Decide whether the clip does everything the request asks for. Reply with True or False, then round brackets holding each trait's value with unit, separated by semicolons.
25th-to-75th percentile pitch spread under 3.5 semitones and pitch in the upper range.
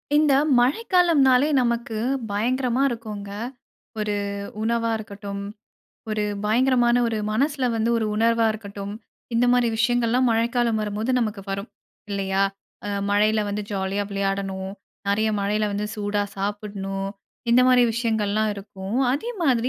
True (3.0 semitones; 220 Hz)